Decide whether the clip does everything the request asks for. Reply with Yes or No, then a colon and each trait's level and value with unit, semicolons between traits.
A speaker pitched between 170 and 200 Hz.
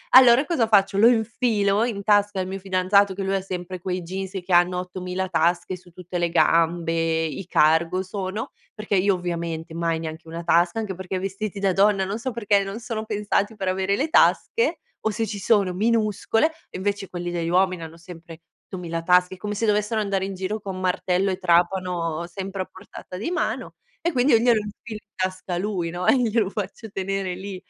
Yes: high, 190 Hz